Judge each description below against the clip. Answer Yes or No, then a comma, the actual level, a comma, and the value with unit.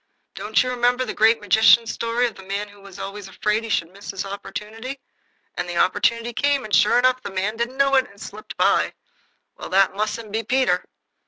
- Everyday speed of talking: No, fast, 215 wpm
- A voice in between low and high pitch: No, high, 220 Hz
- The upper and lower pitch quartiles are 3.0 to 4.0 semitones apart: Yes, average, 3.5 semitones